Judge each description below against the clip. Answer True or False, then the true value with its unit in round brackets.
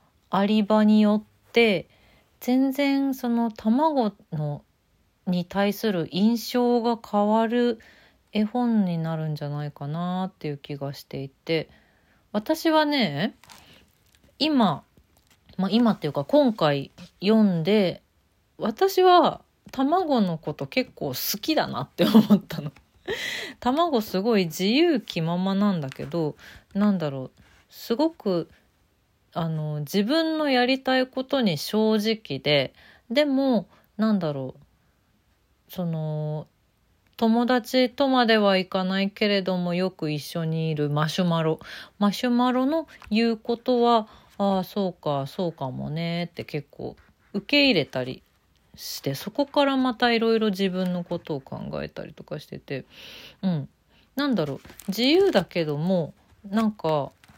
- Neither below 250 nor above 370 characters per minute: False (235 characters per minute)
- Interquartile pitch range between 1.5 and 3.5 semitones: False (7.1 semitones)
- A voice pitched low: False (200 Hz)